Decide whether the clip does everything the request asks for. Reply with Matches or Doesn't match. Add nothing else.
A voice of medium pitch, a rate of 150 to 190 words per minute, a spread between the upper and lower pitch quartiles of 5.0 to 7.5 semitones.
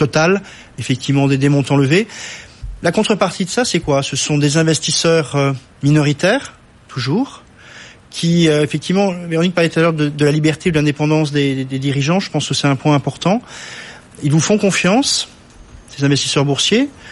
Doesn't match